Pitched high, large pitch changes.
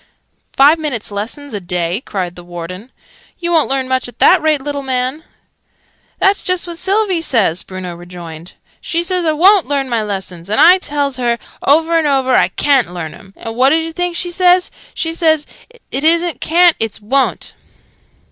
Yes: very high, 275 Hz; wide, 8.2 semitones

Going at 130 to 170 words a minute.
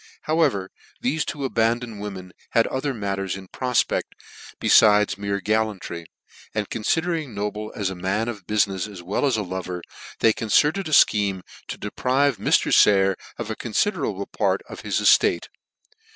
Yes: average, 160 wpm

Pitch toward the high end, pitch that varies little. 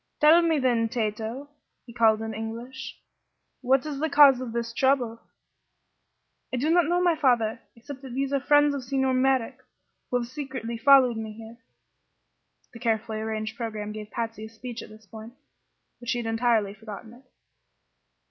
No: high, 240 Hz; average, 3.2 semitones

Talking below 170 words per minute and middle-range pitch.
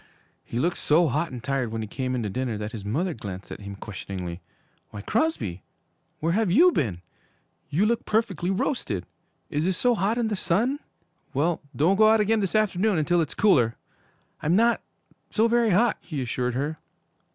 No: average, 185 wpm; medium, 165 Hz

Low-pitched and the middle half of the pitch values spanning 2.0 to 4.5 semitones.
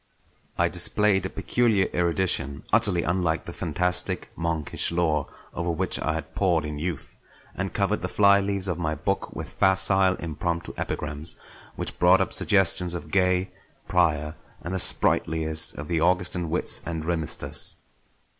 Yes: very low, 85 Hz; average, 2.8 semitones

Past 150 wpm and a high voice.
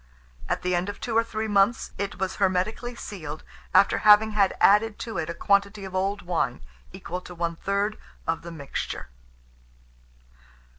Yes: average, 165 wpm; high, 200 Hz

